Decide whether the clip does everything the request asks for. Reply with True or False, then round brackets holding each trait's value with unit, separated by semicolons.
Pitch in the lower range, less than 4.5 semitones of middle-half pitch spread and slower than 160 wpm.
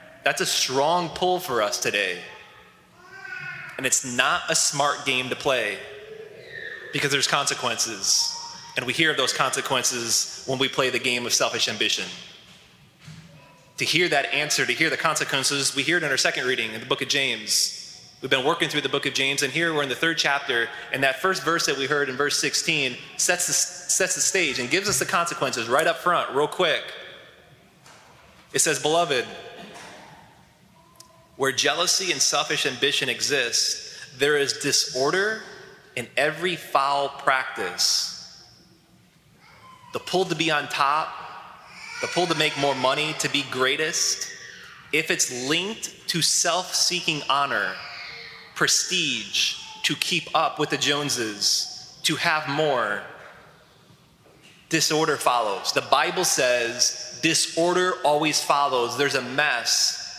False (155 Hz; 4.1 semitones; 150 wpm)